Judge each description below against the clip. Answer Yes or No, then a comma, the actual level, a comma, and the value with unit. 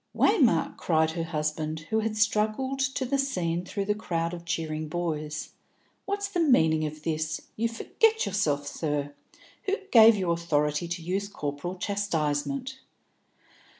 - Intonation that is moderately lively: No, wide, 5.9 semitones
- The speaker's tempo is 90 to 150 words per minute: Yes, average, 145 wpm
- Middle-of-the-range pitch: Yes, medium, 175 Hz